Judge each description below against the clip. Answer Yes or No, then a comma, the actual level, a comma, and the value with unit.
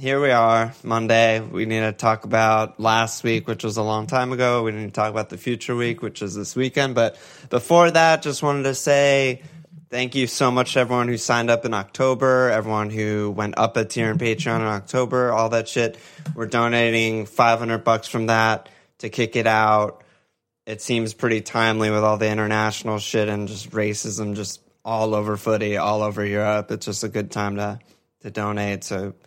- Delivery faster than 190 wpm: Yes, average, 200 wpm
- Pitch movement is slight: Yes, narrow, 2.3 semitones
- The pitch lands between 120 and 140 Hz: No, low, 110 Hz